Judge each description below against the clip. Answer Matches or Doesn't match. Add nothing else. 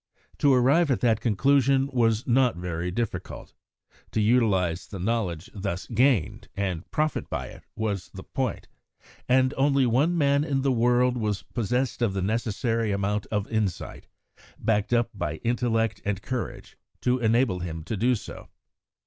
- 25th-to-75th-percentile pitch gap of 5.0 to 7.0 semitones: Doesn't match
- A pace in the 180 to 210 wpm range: Doesn't match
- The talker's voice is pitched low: Matches